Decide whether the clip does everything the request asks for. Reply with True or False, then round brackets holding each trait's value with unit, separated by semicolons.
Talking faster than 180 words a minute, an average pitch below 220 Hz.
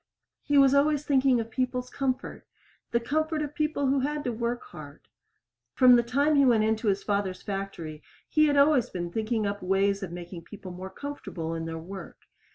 False (190 wpm; 235 Hz)